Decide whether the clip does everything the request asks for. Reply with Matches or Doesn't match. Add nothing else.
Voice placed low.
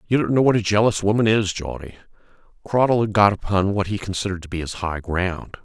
Matches